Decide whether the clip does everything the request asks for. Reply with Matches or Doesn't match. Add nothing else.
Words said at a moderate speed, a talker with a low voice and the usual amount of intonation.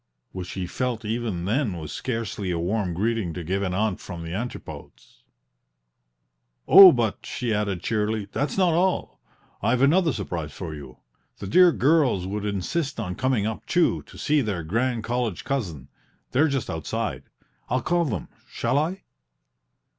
Doesn't match